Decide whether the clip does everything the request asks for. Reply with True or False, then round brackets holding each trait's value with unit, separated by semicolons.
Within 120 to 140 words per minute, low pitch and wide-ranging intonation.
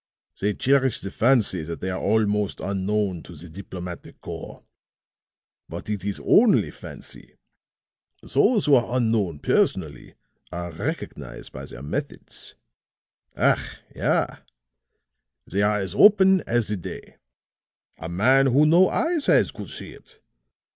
True (135 wpm; 105 Hz; 6.3 semitones)